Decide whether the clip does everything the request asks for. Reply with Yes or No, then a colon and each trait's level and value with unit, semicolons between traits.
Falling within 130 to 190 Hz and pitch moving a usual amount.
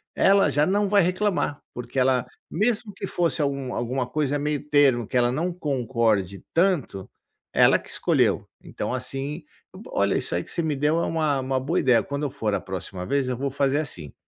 Yes: medium, 140 Hz; average, 4.0 semitones